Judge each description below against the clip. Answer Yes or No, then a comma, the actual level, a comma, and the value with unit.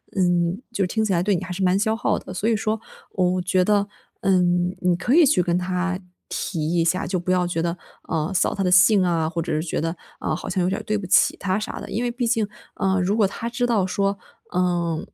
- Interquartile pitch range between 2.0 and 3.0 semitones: Yes, narrow, 2.6 semitones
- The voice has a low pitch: No, medium, 185 Hz